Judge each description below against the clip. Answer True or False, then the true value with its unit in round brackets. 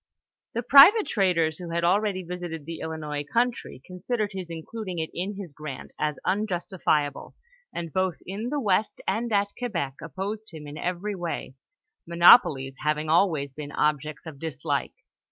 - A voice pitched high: False (175 Hz)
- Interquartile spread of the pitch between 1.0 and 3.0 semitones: False (4.8 semitones)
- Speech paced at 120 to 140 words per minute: False (155 wpm)